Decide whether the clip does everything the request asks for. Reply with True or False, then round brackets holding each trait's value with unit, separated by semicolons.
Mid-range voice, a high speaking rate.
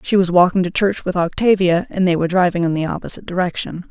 True (180 Hz; 230 wpm)